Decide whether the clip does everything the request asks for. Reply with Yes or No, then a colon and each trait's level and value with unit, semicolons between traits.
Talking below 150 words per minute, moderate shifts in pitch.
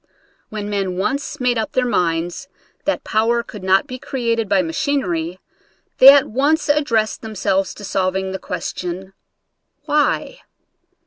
No: average, 140 wpm; wide, 5.9 semitones